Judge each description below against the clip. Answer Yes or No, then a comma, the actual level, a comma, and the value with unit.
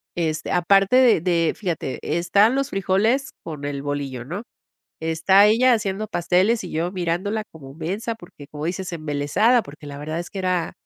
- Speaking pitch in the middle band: Yes, medium, 175 Hz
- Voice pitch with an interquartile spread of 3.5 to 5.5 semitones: Yes, average, 4.7 semitones